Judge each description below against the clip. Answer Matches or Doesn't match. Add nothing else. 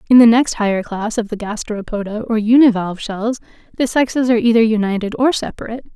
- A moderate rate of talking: Matches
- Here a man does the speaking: Doesn't match